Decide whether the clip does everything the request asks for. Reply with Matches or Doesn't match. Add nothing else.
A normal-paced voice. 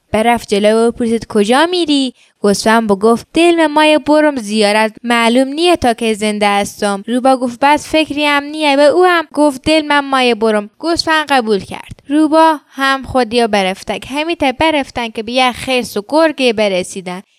Doesn't match